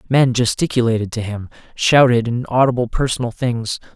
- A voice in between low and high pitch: No, low, 120 Hz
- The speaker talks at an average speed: No, slow, 120 wpm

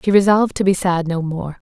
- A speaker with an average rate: No, fast, 250 wpm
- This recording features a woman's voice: Yes, female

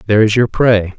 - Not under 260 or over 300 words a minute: No, fast, 245 wpm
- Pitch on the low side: Yes, low, 110 Hz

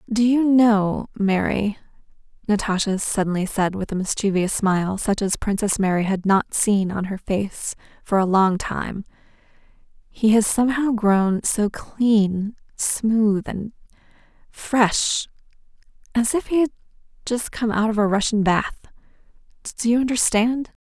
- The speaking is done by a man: No, female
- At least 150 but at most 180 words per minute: No, slow, 135 wpm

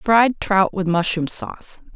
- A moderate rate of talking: Yes, average, 155 wpm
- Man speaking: No, female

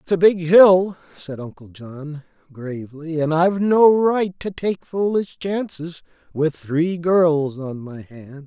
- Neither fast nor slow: Yes, average, 155 wpm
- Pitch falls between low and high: Yes, medium, 165 Hz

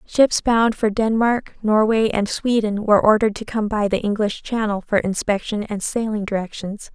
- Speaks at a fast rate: No, average, 175 wpm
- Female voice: Yes, female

